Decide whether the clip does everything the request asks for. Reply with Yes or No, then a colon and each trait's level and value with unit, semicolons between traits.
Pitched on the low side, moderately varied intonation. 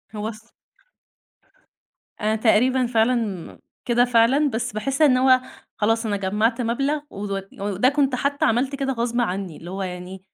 No: high, 230 Hz; average, 3.6 semitones